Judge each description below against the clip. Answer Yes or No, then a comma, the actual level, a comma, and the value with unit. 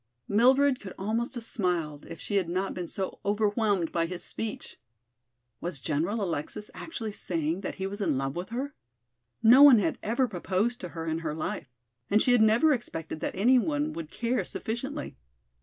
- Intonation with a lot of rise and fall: Yes, wide, 5.9 semitones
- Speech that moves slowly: No, average, 185 wpm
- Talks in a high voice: Yes, high, 205 Hz